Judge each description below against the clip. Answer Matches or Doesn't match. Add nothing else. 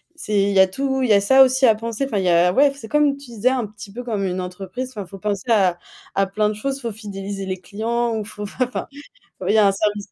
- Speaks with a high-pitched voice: Matches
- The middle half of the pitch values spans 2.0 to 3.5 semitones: Doesn't match